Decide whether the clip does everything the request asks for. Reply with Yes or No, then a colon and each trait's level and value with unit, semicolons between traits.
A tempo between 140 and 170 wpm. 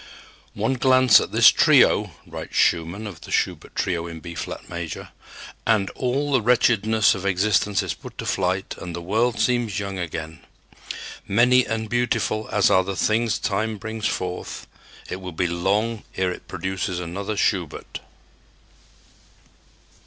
Yes: average, 150 wpm